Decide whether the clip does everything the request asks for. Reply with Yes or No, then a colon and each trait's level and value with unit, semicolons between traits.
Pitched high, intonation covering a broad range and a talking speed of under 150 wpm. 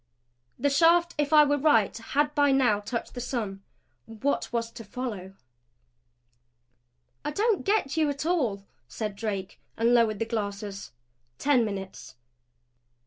Yes: high, 240 Hz; wide, 5.7 semitones; average, 140 wpm